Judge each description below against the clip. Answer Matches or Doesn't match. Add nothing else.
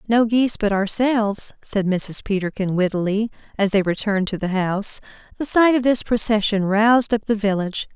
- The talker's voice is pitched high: Matches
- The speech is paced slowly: Doesn't match